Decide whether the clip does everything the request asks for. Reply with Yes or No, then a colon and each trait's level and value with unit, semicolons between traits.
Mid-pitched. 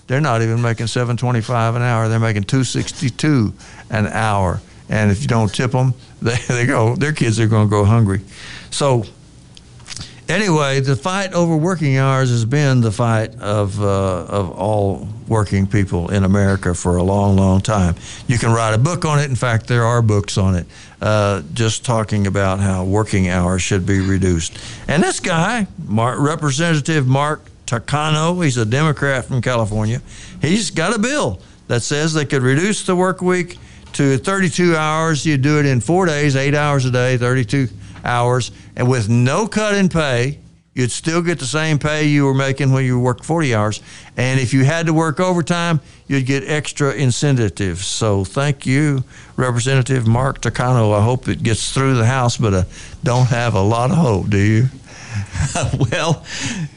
No: low, 125 Hz